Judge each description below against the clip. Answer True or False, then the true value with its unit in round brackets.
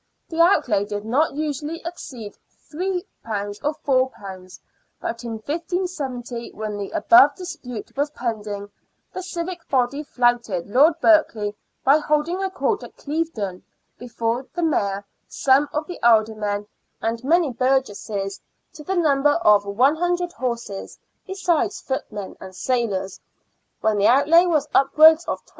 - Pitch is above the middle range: True (265 Hz)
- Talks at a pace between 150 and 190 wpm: False (135 wpm)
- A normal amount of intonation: False (6.9 semitones)